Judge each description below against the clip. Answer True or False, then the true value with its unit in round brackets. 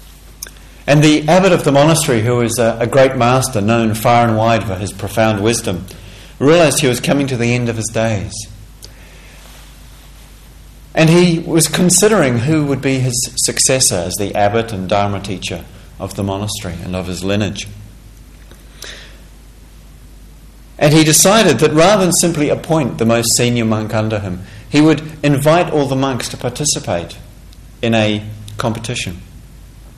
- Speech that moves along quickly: False (155 wpm)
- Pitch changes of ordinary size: False (5.7 semitones)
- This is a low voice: True (115 Hz)